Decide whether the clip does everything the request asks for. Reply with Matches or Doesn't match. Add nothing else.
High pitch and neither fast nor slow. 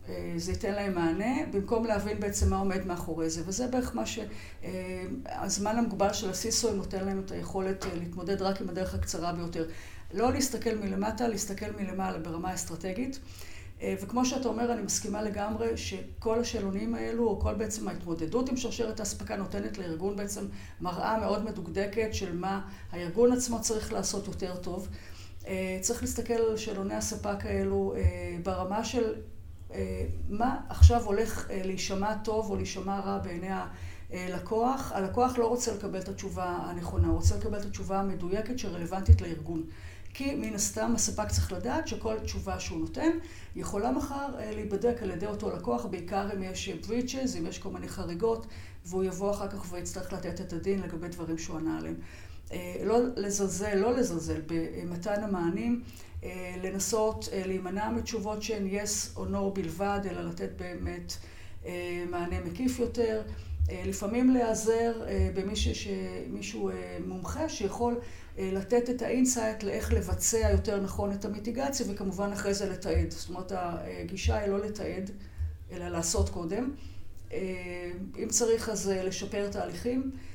Matches